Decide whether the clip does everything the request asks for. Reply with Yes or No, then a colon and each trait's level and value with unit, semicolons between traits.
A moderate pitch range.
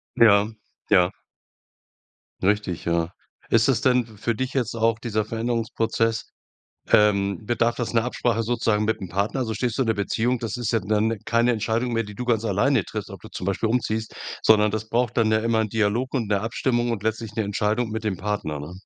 No: narrow, 2.1 semitones